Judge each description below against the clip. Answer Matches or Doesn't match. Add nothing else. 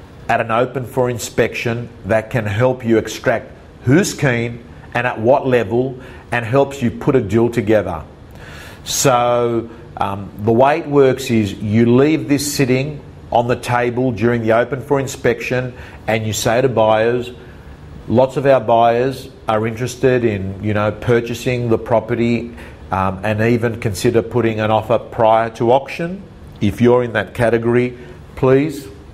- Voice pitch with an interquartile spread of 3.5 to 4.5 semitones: Doesn't match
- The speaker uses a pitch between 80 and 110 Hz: Doesn't match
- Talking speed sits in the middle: Matches